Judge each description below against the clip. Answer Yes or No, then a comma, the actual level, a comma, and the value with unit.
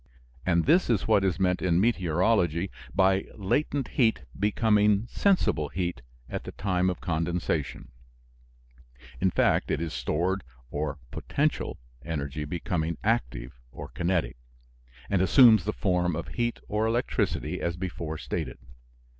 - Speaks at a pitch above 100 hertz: No, very low, 90 Hz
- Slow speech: Yes, slow, 130 wpm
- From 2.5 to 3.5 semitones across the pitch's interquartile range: No, average, 4.2 semitones